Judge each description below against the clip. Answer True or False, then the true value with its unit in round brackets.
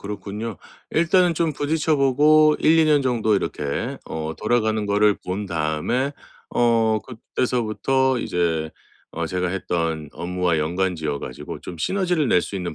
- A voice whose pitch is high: False (105 Hz)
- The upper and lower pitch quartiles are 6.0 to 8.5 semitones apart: True (7.5 semitones)